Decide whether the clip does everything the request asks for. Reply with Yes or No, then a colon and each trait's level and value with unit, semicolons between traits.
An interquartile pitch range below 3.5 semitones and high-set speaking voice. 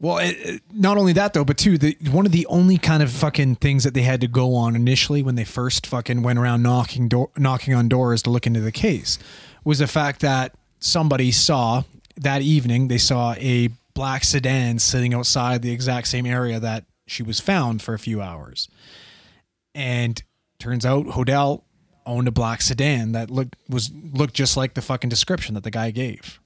No: average, 2.9 semitones; low, 125 Hz